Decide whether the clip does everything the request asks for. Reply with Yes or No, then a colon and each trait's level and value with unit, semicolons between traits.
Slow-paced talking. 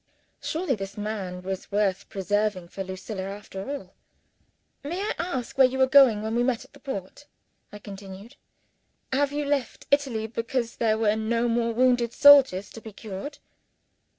No: average, 165 wpm